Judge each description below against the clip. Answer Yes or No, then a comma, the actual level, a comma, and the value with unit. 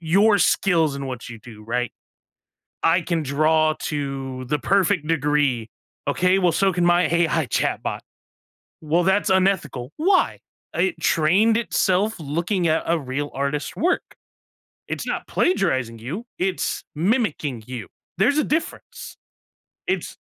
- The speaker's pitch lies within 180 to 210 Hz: No, medium, 165 Hz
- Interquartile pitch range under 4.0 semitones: No, wide, 5.6 semitones